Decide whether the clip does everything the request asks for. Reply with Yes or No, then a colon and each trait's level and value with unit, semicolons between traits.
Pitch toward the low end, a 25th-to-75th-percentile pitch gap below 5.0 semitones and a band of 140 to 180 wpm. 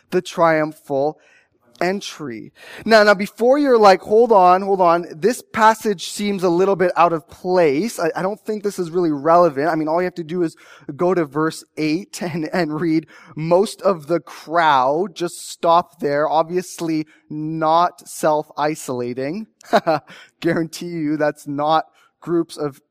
No: medium, 170 Hz; average, 2.9 semitones; average, 155 wpm